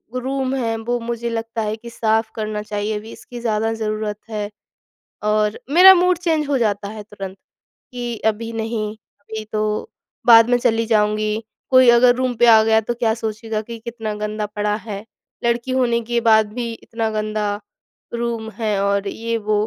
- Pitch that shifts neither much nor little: No, narrow, 1.9 semitones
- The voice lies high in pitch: Yes, high, 225 Hz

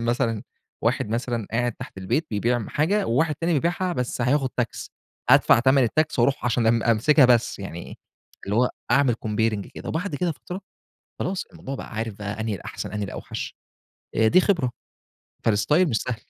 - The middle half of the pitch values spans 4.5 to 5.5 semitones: Yes, average, 5.0 semitones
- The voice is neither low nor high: No, low, 120 Hz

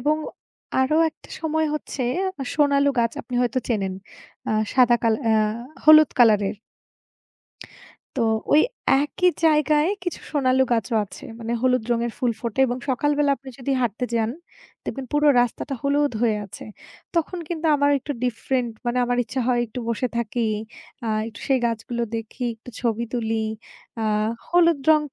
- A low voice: No, very high, 250 Hz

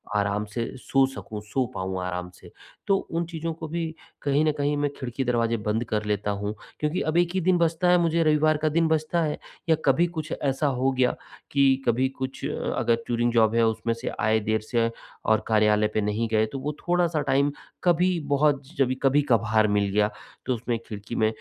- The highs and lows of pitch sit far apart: Yes, wide, 6.1 semitones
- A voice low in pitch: Yes, low, 130 Hz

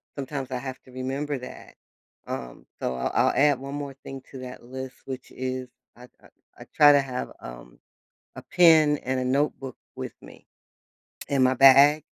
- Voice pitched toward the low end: Yes, low, 130 Hz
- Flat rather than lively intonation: Yes, narrow, 1.8 semitones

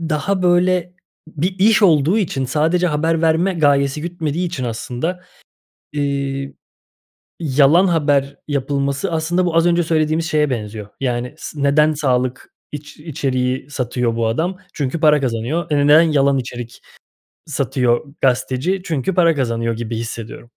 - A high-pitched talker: No, medium, 145 Hz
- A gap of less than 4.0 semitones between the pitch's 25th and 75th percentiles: No, average, 4.3 semitones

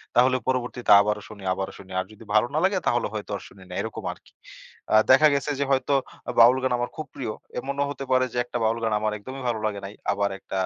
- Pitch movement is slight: No, average, 3.7 semitones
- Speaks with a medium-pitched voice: No, low, 120 Hz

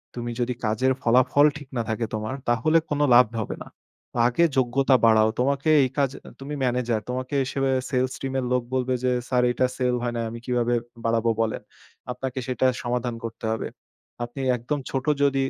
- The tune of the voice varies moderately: No, narrow, 2.0 semitones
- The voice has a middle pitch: No, low, 125 Hz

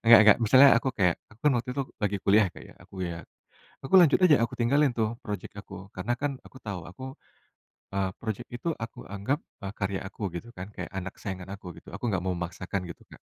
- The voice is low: Yes, low, 105 Hz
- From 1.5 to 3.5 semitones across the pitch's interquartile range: No, average, 4.2 semitones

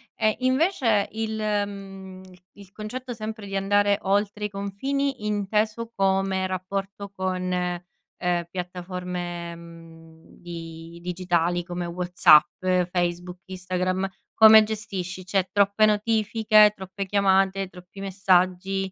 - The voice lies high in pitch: Yes, high, 195 Hz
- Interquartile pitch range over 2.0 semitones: Yes, average, 2.7 semitones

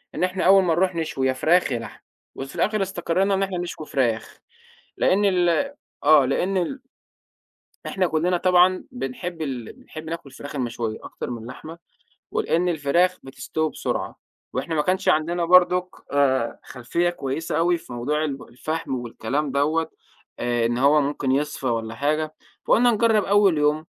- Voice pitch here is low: No, medium, 155 Hz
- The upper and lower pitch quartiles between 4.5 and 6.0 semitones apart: Yes, average, 5.2 semitones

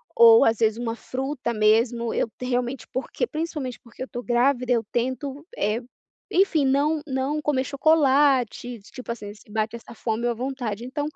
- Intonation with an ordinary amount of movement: Yes, average, 3.2 semitones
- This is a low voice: No, very high, 255 Hz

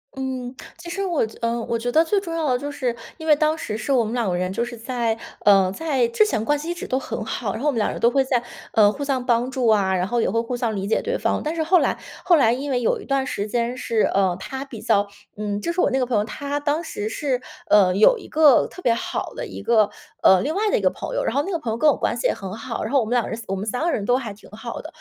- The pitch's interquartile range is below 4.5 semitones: No, average, 4.9 semitones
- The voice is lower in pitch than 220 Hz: No, high, 245 Hz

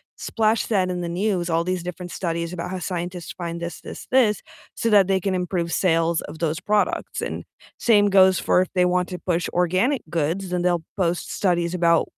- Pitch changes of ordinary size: No, narrow, 2.0 semitones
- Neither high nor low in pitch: Yes, medium, 180 Hz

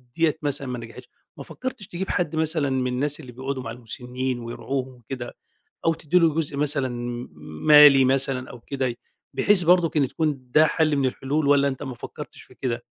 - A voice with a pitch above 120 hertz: Yes, low, 135 Hz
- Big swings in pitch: No, average, 3.3 semitones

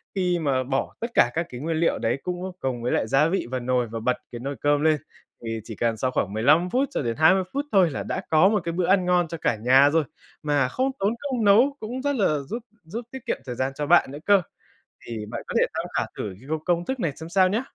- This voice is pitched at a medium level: Yes, medium, 160 Hz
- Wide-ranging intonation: Yes, wide, 6.9 semitones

